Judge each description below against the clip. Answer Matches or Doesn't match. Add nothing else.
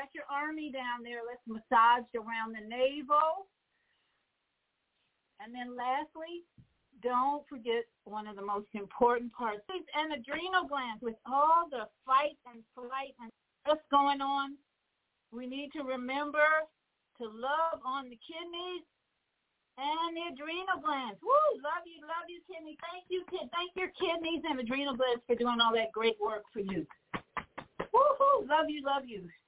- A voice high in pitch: Matches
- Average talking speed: Matches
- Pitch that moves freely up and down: Doesn't match